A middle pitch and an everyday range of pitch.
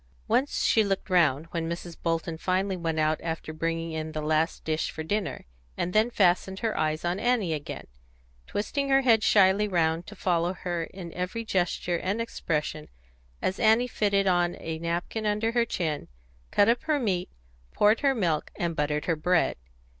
Yes: medium, 180 Hz; average, 4.4 semitones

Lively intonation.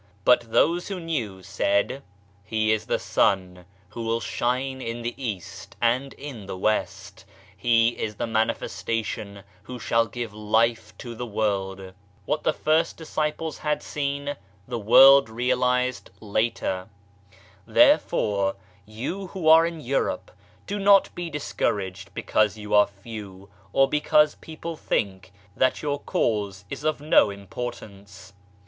Yes: wide, 5.8 semitones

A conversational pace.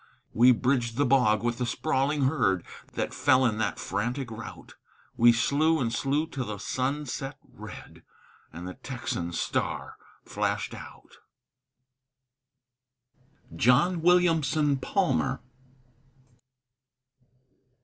No: slow, 110 wpm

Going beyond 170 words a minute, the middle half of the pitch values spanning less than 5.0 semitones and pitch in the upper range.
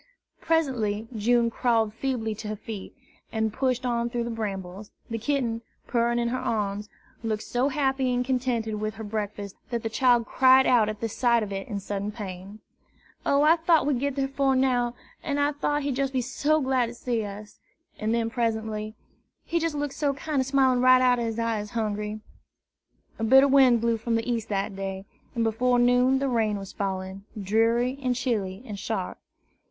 Yes: average, 190 wpm; average, 3.4 semitones; high, 235 Hz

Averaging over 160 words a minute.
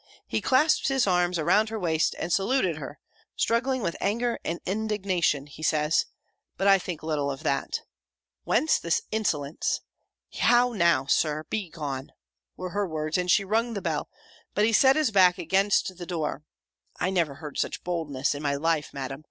Yes: average, 170 wpm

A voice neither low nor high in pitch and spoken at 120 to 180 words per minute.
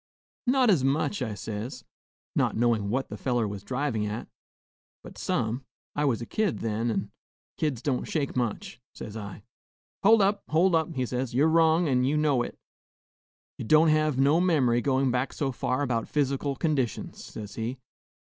No: low, 130 Hz; average, 175 wpm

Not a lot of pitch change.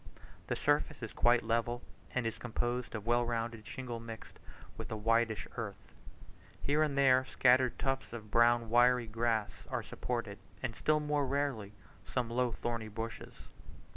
Yes: narrow, 2.0 semitones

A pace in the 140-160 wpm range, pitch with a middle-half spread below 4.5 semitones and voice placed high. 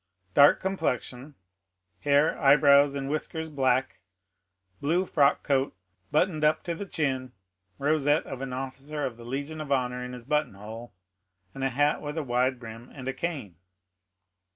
No: average, 150 wpm; average, 3.0 semitones; medium, 140 Hz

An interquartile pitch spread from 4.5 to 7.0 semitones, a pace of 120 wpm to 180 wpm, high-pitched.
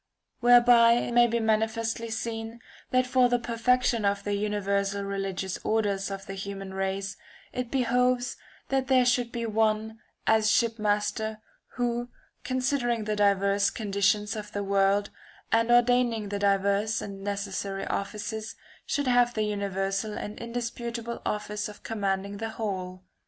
No: average, 2.9 semitones; average, 140 wpm; high, 215 Hz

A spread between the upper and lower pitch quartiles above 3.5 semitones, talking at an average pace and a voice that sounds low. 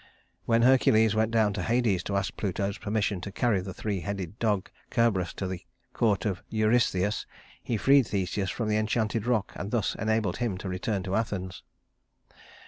No: average, 2.7 semitones; average, 175 wpm; low, 105 Hz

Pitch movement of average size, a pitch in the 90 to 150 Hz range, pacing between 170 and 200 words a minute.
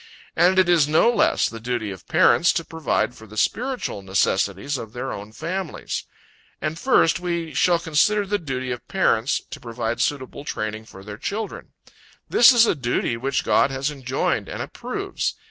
No: wide, 7.2 semitones; medium, 140 Hz; average, 175 wpm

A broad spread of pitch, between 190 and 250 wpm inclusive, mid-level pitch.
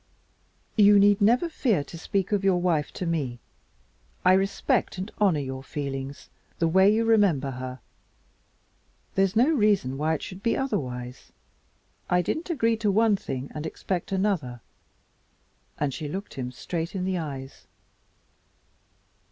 No: wide, 6.5 semitones; average, 150 wpm; medium, 180 Hz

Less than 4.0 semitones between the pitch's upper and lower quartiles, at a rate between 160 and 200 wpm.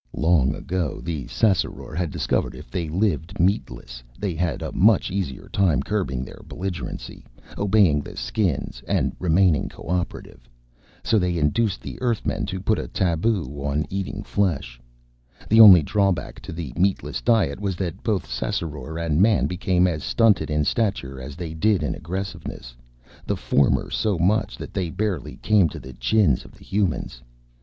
No: average, 4.7 semitones; average, 165 wpm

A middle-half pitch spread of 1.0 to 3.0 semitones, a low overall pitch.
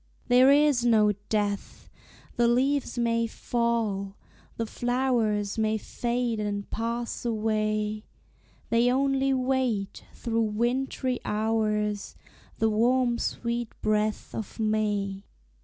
No: narrow, 2.4 semitones; high, 230 Hz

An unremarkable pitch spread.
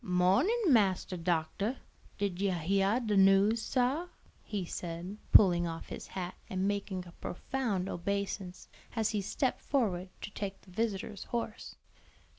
Yes: average, 3.3 semitones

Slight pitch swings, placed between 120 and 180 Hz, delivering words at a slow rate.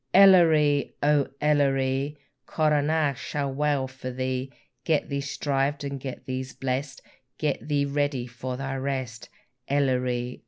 Yes: narrow, 2.0 semitones; medium, 140 Hz; slow, 125 wpm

